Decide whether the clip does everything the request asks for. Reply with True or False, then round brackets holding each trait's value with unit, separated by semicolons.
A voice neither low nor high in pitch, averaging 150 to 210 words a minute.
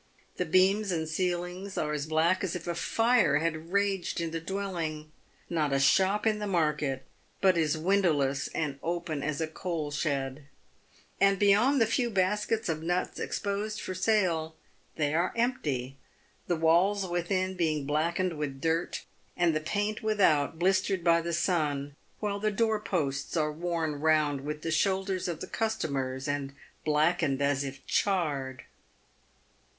True (170 Hz; 160 wpm)